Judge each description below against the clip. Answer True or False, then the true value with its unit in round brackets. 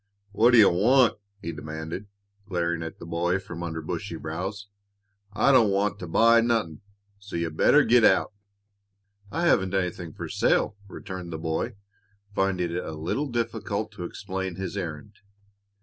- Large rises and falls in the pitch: False (4.2 semitones)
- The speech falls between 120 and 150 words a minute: False (160 wpm)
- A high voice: False (95 Hz)